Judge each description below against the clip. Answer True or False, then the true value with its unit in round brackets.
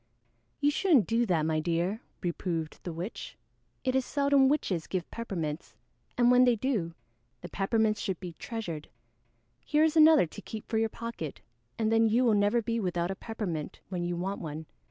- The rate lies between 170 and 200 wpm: True (180 wpm)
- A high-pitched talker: True (210 Hz)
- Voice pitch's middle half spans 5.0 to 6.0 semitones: True (5.6 semitones)